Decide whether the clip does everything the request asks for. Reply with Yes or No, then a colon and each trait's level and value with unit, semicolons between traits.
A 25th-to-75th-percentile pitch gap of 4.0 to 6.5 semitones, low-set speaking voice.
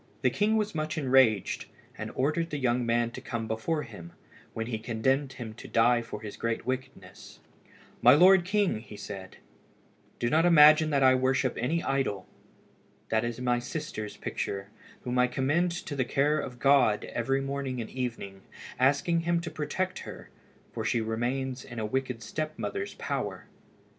Yes: average, 4.7 semitones; low, 130 Hz